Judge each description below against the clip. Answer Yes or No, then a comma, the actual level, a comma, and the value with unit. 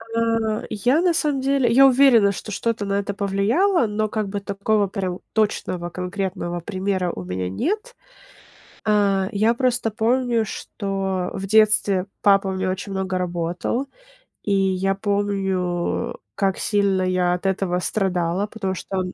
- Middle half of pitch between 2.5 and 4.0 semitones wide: Yes, average, 2.9 semitones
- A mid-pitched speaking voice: No, high, 200 Hz